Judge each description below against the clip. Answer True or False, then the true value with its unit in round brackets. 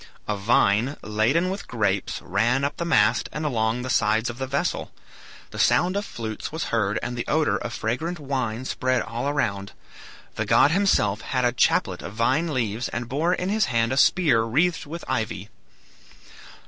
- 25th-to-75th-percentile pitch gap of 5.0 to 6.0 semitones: True (5.6 semitones)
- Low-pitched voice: True (125 Hz)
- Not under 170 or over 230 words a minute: True (180 wpm)